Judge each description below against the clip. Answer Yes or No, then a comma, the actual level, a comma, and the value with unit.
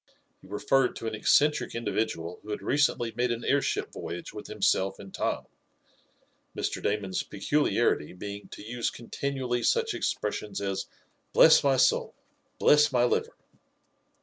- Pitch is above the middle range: No, low, 115 Hz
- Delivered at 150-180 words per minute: No, average, 140 wpm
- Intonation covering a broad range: No, average, 4.0 semitones